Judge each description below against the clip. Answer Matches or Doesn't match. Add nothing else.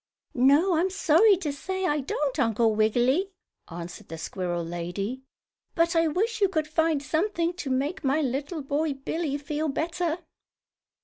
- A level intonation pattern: Doesn't match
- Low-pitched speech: Doesn't match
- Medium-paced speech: Matches